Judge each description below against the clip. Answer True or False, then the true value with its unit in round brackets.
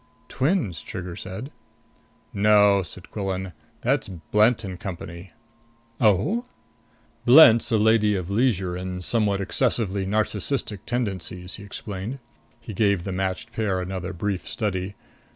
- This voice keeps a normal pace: False (120 wpm)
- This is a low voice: True (100 Hz)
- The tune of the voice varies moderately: True (3.0 semitones)